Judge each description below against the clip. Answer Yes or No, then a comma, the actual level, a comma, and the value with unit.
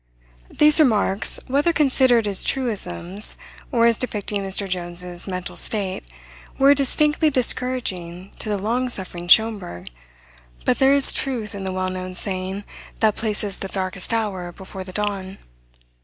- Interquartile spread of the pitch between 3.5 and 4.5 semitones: No, average, 4.9 semitones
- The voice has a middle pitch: No, high, 205 Hz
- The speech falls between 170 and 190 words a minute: No, average, 140 wpm